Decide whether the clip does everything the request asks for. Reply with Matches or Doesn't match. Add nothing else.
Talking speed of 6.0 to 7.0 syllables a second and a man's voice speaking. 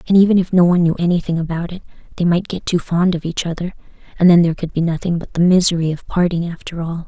Doesn't match